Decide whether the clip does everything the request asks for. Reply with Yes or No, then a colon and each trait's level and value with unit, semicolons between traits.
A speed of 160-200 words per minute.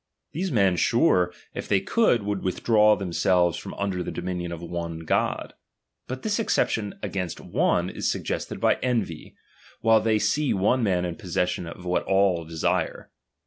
Yes: average, 165 wpm